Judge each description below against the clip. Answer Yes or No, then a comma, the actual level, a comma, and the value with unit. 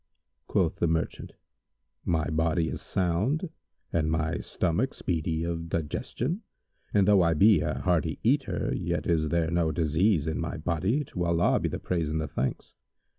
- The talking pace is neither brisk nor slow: Yes, average, 165 wpm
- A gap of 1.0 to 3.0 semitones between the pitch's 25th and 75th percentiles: Yes, average, 2.7 semitones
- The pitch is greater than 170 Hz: No, very low, 85 Hz